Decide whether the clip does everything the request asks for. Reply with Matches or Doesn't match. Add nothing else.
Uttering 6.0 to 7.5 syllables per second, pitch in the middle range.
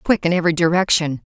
Matches